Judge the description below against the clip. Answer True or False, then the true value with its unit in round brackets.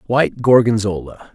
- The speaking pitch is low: True (110 Hz)